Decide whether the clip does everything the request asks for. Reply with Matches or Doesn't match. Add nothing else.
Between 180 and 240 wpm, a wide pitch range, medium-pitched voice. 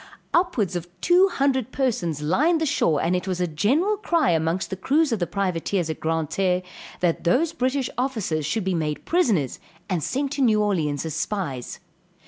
Doesn't match